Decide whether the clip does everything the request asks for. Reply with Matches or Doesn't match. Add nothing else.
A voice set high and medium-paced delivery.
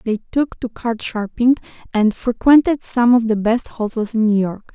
Matches